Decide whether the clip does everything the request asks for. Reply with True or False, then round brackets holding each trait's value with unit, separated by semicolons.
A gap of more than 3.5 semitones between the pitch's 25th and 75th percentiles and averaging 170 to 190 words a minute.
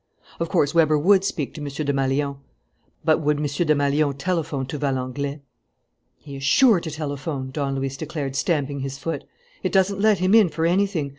False (3.2 semitones; 175 wpm)